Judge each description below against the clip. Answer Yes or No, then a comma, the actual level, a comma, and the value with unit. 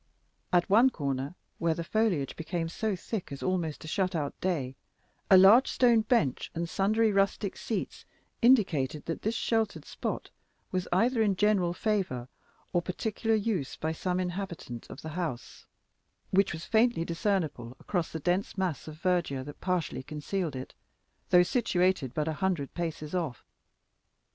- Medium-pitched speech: Yes, medium, 180 Hz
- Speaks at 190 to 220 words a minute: No, average, 155 wpm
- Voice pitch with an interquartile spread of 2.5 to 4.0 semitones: No, average, 4.5 semitones